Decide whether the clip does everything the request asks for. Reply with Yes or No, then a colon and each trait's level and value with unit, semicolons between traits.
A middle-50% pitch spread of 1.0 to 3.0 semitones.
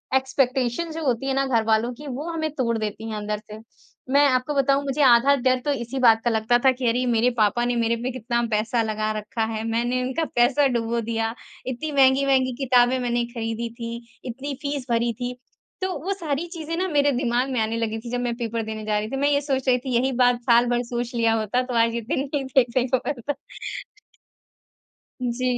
Yes: average, 2.7 semitones